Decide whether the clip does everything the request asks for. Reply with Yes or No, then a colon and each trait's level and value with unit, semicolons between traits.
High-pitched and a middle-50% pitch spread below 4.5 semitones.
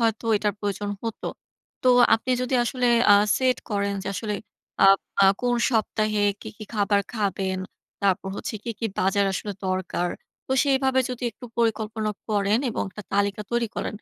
Yes: high, 215 Hz; narrow, 2.6 semitones